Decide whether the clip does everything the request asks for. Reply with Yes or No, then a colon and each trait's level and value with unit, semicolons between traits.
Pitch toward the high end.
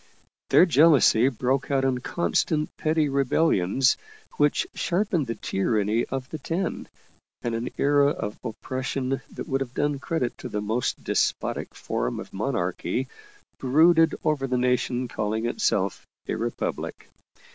No: low, 135 Hz